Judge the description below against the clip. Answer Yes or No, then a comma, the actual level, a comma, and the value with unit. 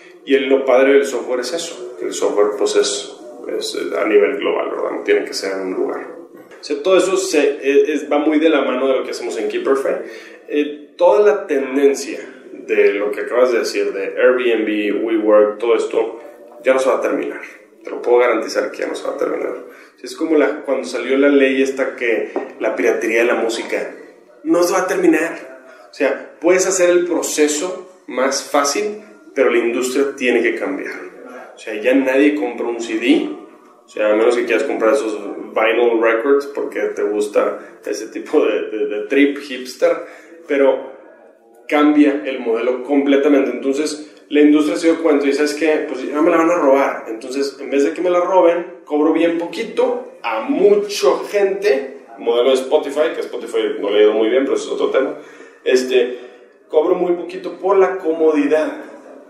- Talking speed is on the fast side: Yes, fast, 195 wpm